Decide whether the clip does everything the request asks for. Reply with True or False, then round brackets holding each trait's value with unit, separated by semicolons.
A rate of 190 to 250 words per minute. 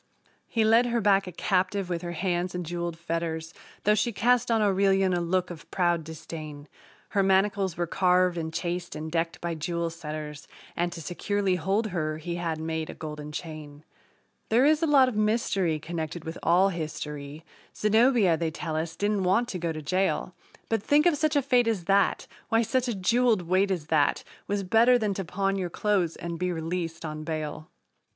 True (195 wpm)